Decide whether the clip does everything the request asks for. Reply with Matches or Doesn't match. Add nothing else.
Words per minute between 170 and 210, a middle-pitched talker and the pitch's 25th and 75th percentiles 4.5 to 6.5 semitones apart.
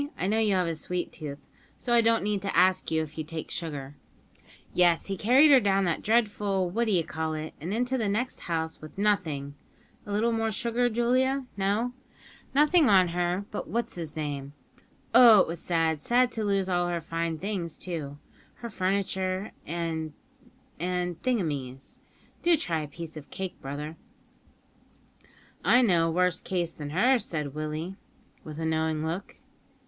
Matches